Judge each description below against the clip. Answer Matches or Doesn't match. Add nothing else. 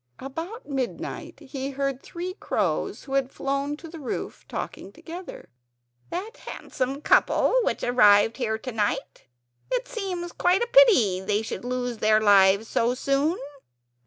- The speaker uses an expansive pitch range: Matches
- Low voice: Doesn't match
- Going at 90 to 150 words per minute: Matches